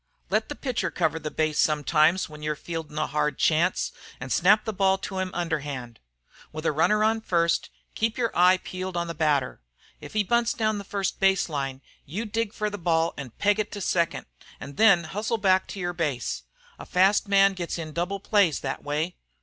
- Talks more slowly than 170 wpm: No, fast, 205 wpm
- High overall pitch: No, medium, 175 Hz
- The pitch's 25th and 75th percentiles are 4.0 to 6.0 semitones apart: Yes, average, 4.8 semitones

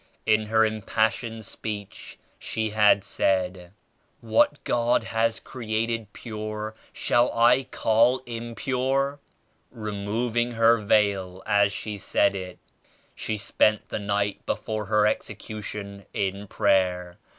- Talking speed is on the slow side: Yes, slow, 115 wpm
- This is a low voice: Yes, low, 110 Hz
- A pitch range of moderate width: No, narrow, 2.2 semitones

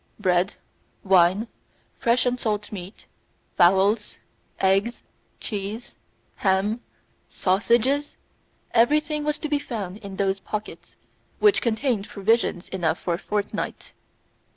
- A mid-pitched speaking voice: No, high, 210 Hz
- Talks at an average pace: No, slow, 105 wpm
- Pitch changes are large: No, average, 3.8 semitones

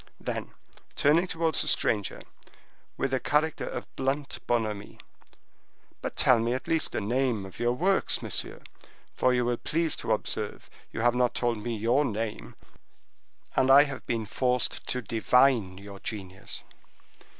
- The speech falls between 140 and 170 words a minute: Yes, average, 150 wpm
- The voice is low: Yes, low, 120 Hz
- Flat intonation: No, average, 3.7 semitones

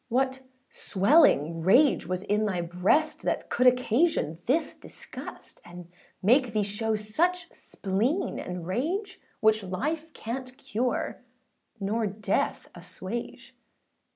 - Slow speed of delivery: Yes, slow, 115 wpm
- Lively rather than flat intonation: Yes, wide, 5.9 semitones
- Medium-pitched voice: No, high, 220 Hz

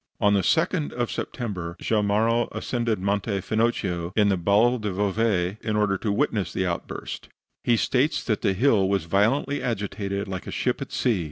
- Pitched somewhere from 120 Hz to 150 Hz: No, low, 105 Hz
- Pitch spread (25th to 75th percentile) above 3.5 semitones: No, average, 3.2 semitones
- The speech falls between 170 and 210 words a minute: Yes, average, 175 wpm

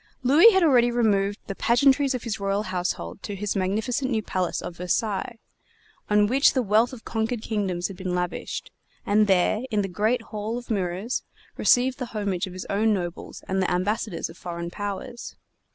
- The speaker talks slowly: No, average, 185 wpm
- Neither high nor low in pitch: No, high, 210 Hz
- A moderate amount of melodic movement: Yes, average, 4.1 semitones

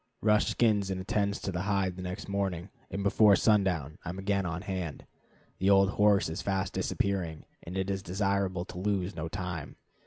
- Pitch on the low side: Yes, very low, 95 Hz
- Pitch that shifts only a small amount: Yes, narrow, 1.8 semitones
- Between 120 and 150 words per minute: No, average, 190 wpm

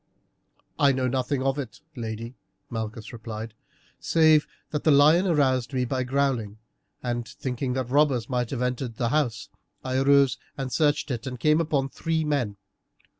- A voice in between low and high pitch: No, low, 130 Hz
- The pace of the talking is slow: No, average, 160 wpm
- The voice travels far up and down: No, average, 3.1 semitones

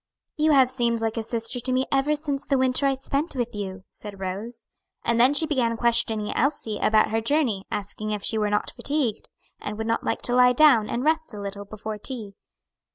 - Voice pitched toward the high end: Yes, high, 235 Hz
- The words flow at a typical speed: No, fast, 215 wpm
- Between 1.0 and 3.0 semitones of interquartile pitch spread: No, average, 4.1 semitones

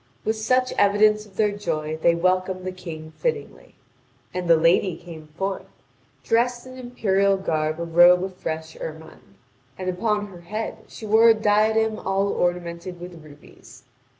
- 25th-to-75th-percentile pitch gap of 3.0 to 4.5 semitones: Yes, average, 4.1 semitones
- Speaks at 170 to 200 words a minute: No, average, 155 wpm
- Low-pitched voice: No, medium, 185 Hz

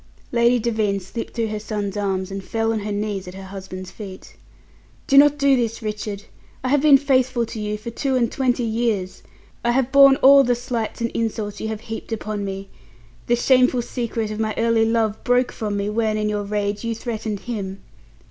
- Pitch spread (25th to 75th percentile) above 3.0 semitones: No, average, 2.7 semitones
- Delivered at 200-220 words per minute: Yes, fast, 205 wpm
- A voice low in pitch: No, high, 225 Hz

